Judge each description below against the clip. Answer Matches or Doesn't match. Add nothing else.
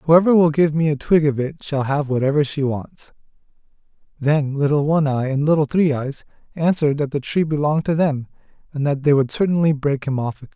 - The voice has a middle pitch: Matches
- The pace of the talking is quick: Matches